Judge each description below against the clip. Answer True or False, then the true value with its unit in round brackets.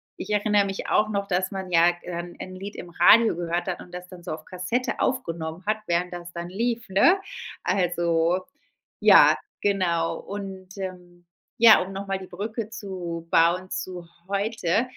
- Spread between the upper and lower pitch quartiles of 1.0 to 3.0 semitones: True (2.6 semitones)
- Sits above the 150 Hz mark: True (185 Hz)